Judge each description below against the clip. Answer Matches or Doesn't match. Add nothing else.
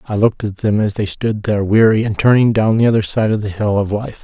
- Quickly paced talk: Matches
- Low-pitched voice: Matches